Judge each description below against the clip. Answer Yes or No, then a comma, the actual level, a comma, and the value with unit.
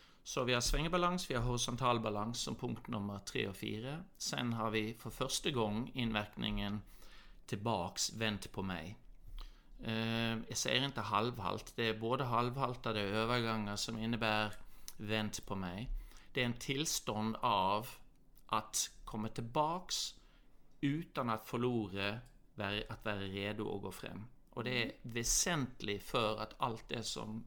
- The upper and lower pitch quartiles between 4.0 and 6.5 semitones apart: No, average, 2.7 semitones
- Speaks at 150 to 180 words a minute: No, average, 140 wpm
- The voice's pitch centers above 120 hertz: No, low, 115 Hz